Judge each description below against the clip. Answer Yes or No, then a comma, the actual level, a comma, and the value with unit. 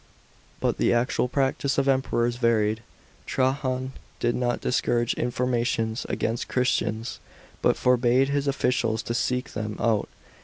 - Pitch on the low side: Yes, low, 120 Hz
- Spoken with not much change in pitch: Yes, narrow, 1.9 semitones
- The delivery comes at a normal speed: No, slow, 130 wpm